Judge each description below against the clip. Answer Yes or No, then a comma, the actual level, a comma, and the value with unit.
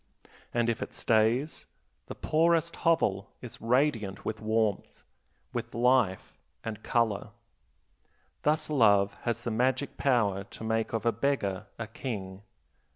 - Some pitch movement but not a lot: Yes, average, 3.7 semitones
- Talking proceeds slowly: Yes, slow, 130 wpm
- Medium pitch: No, low, 115 Hz